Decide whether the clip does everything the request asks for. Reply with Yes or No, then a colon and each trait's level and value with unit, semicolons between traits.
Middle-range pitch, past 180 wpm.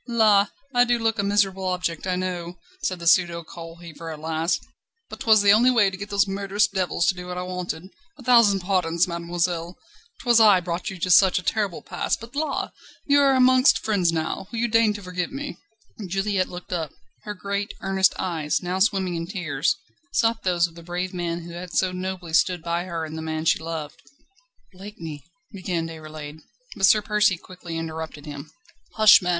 Yes: medium, 180 Hz; average, 200 wpm